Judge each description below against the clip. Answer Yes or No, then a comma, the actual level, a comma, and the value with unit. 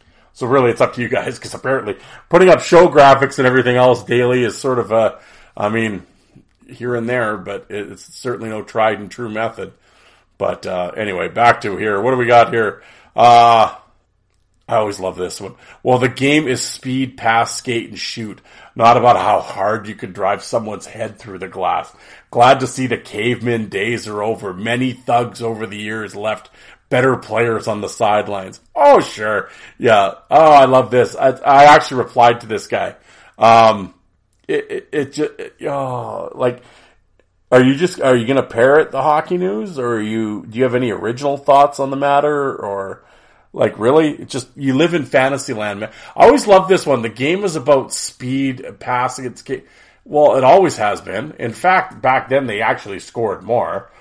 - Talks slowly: No, average, 190 wpm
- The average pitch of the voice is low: Yes, low, 125 Hz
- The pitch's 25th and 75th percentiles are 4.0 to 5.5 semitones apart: No, average, 3.5 semitones